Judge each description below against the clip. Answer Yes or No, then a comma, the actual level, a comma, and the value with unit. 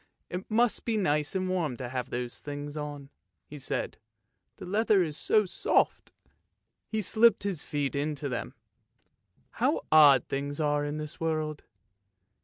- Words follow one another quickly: No, average, 170 wpm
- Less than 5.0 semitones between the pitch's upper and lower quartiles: Yes, average, 4.5 semitones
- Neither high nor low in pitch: Yes, medium, 150 Hz